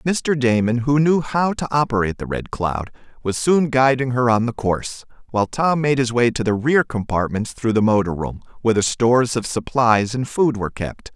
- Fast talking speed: Yes, fast, 210 wpm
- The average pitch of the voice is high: No, low, 120 Hz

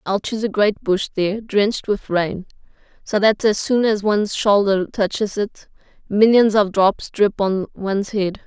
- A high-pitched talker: Yes, high, 205 Hz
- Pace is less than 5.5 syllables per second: Yes, 4.6 syllables/s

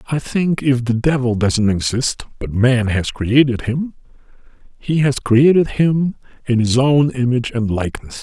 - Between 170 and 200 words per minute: No, average, 160 wpm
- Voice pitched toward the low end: Yes, low, 130 Hz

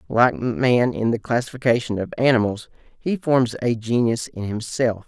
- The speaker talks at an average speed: Yes, average, 155 wpm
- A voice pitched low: Yes, low, 120 Hz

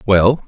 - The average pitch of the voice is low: Yes, low, 110 Hz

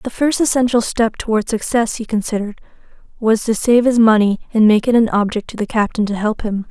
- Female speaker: Yes, female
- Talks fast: Yes, fast, 215 wpm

